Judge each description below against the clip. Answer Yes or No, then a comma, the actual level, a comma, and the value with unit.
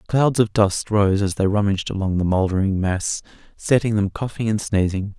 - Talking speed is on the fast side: No, average, 185 wpm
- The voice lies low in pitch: Yes, low, 100 Hz